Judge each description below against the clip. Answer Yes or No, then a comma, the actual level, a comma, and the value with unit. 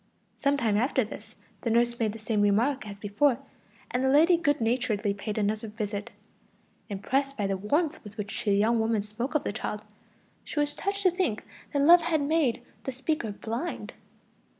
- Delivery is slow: No, average, 185 wpm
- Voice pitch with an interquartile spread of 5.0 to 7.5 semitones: Yes, average, 5.3 semitones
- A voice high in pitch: Yes, high, 235 Hz